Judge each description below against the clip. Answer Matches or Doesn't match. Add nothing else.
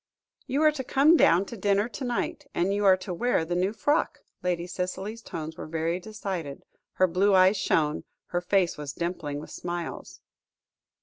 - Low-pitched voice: Doesn't match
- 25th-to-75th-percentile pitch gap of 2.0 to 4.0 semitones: Matches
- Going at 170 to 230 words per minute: Matches